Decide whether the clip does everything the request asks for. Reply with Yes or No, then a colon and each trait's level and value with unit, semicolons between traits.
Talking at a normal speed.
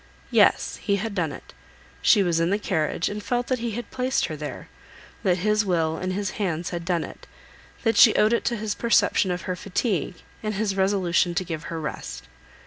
No: fast, 210 wpm